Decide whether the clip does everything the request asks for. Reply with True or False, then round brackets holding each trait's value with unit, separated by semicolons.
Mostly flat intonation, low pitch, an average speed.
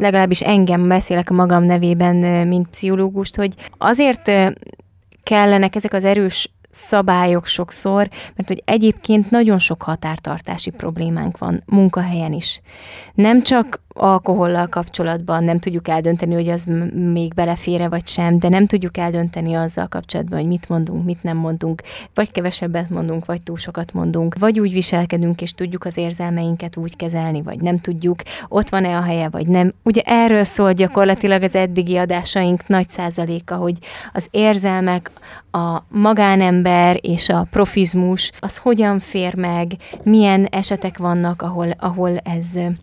False (2.2 semitones; 180 Hz; 145 wpm)